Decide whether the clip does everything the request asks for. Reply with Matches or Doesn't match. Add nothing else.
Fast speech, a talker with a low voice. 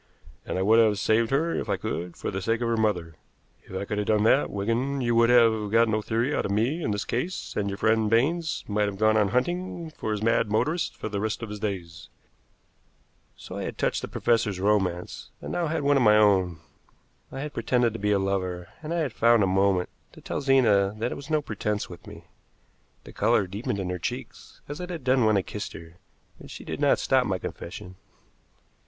Matches